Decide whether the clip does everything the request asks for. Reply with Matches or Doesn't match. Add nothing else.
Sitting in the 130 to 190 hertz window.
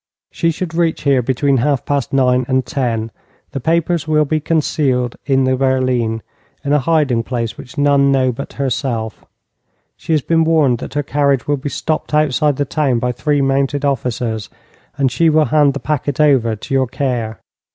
Matches